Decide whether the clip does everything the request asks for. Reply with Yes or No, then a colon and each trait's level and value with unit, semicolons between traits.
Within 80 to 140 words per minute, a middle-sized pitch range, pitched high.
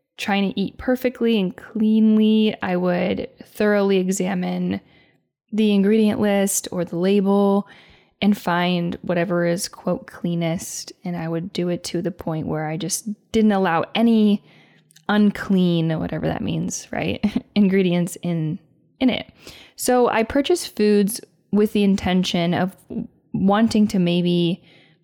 Yes: slow, 135 wpm; average, 3.5 semitones; high, 195 Hz